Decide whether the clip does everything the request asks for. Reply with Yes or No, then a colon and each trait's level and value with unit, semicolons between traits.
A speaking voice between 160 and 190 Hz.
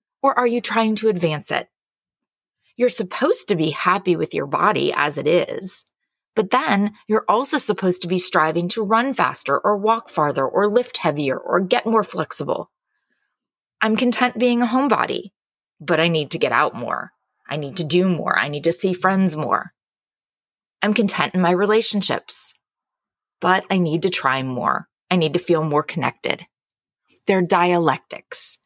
Yes: medium, 185 Hz